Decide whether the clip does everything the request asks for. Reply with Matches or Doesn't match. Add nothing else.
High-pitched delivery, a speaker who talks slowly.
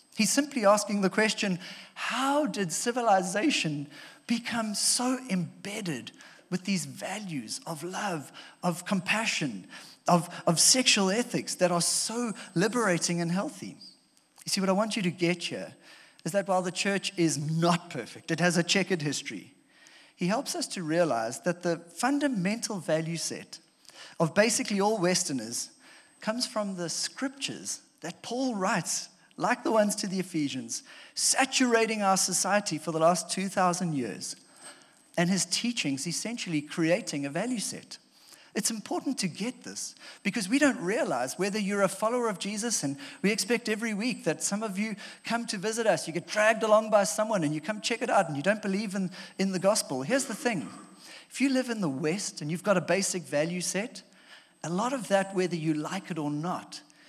Doesn't match